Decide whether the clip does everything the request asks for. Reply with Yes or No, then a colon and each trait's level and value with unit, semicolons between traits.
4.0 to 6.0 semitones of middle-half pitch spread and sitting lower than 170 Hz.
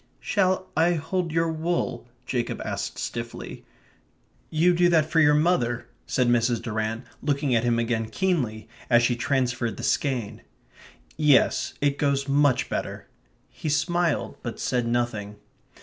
Yes: average, 5.2 semitones; medium, 140 Hz